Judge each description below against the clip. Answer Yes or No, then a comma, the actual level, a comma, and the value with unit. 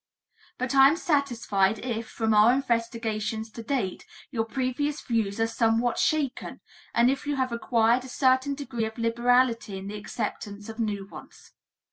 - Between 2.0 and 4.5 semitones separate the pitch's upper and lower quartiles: Yes, average, 2.8 semitones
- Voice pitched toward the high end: Yes, high, 235 Hz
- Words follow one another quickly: No, average, 160 wpm